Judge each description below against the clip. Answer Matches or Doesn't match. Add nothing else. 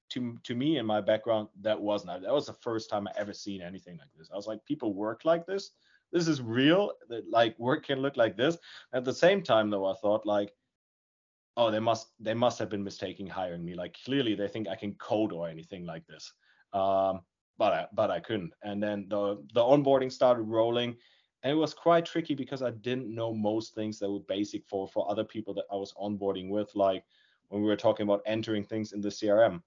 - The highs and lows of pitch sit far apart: Doesn't match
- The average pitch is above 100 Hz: Matches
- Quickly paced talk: Matches